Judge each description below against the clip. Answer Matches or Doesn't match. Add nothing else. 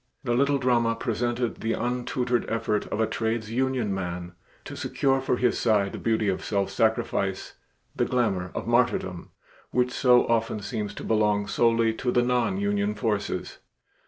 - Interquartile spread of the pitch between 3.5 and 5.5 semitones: Doesn't match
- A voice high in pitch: Doesn't match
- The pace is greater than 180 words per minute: Doesn't match